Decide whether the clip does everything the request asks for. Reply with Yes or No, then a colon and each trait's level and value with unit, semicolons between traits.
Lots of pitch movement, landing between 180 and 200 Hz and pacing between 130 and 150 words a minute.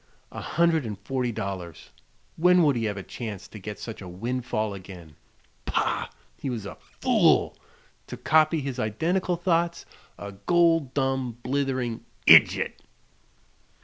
No: wide, 7.4 semitones; low, 125 Hz; average, 140 wpm